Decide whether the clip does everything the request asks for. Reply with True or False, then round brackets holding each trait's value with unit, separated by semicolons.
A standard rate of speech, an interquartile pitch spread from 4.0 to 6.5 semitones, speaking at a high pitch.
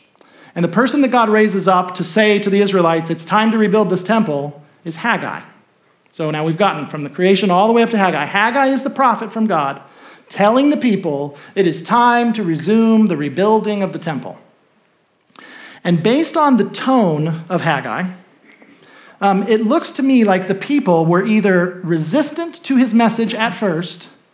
True (185 wpm; 5.1 semitones; 200 Hz)